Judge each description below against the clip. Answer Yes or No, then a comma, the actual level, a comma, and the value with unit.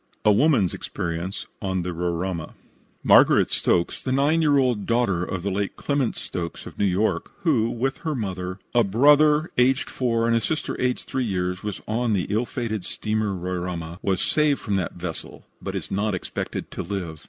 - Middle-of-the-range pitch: No, low, 105 Hz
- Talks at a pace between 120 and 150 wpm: No, average, 185 wpm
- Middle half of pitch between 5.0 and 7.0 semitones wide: Yes, wide, 5.6 semitones